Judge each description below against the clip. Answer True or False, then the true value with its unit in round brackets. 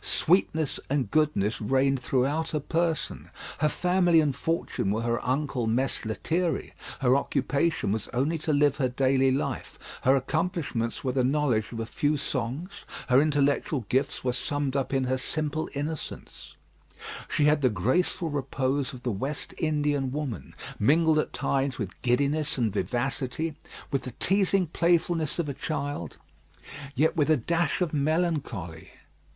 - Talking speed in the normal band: True (150 wpm)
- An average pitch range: True (3.5 semitones)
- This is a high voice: False (140 Hz)